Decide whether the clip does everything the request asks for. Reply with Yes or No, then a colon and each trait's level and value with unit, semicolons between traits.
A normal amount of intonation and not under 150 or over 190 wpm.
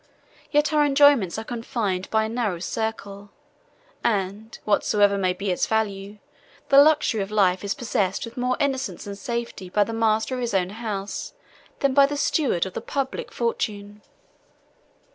Yes: average, 4.0 semitones; average, 160 wpm